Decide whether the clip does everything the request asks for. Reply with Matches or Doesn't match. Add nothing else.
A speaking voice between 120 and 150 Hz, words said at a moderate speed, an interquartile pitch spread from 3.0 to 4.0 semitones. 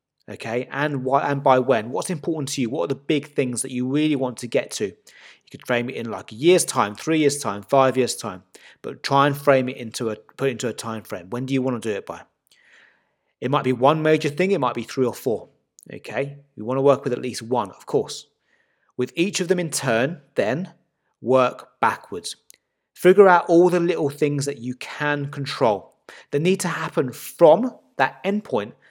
Doesn't match